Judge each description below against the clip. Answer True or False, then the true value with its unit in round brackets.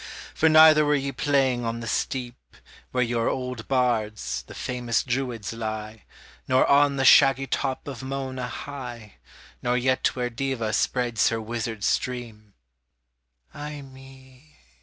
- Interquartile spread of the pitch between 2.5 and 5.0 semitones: True (2.8 semitones)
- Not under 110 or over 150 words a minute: True (140 wpm)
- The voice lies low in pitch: True (125 Hz)